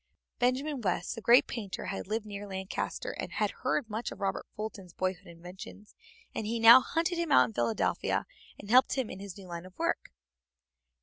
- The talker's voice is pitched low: No, high, 205 Hz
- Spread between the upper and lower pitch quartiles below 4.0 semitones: No, average, 4.3 semitones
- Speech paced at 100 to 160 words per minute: No, average, 190 wpm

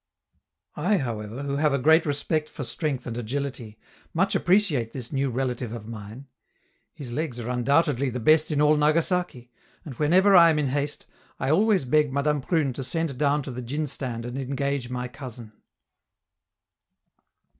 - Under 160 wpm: No, average, 165 wpm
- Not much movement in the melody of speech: No, average, 3.8 semitones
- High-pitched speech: No, medium, 140 Hz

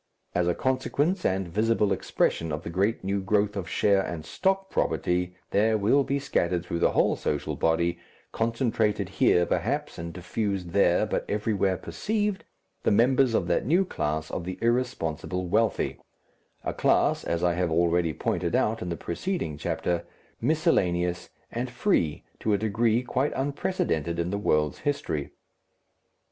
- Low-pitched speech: Yes, low, 100 Hz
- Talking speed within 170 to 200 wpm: No, average, 155 wpm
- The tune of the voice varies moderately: No, wide, 5.8 semitones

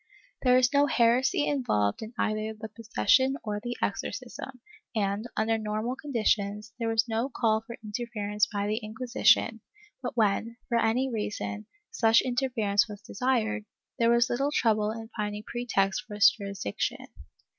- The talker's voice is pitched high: Yes, high, 225 Hz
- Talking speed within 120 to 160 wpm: Yes, average, 155 wpm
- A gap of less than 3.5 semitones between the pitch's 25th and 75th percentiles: Yes, narrow, 2.5 semitones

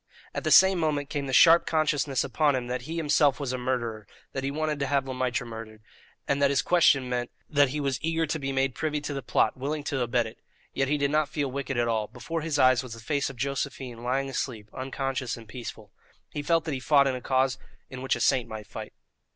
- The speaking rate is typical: No, fast, 240 wpm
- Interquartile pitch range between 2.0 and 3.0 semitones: Yes, average, 2.7 semitones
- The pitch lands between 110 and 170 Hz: Yes, low, 135 Hz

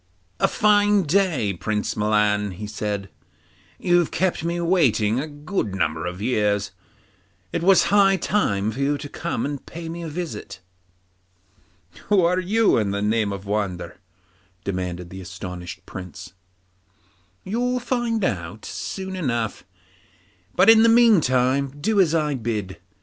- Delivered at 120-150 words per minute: Yes, average, 145 wpm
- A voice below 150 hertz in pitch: Yes, low, 135 Hz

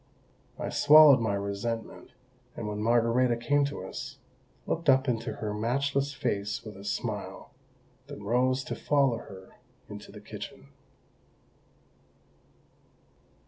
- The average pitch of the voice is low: Yes, low, 120 Hz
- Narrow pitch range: No, average, 4.7 semitones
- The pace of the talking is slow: Yes, slow, 120 wpm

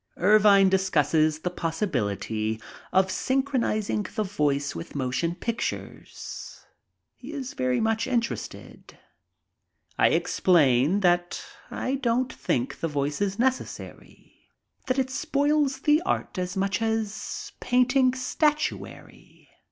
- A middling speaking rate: No, slow, 115 wpm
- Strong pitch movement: Yes, wide, 8.0 semitones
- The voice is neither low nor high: No, high, 205 Hz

